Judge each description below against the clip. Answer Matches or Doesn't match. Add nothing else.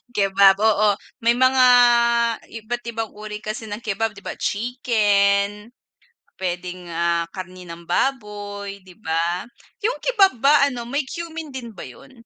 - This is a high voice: Matches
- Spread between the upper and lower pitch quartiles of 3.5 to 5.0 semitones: Matches